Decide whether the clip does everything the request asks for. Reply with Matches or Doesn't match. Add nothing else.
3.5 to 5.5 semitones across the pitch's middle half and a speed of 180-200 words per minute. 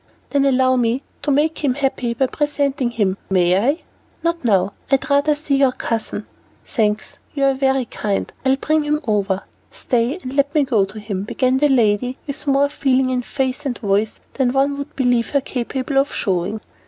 Matches